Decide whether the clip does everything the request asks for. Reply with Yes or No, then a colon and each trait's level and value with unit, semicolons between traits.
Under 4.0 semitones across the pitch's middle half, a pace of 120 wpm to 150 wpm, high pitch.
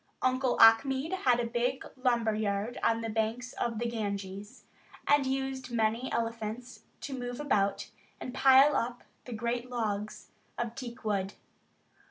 Yes: average, 2.8 semitones; average, 145 wpm; high, 235 Hz